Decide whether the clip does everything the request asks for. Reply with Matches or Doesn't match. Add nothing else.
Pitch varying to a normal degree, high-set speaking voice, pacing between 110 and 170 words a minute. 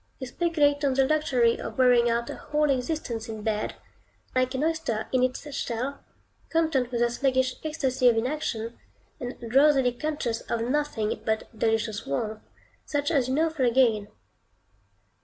Matches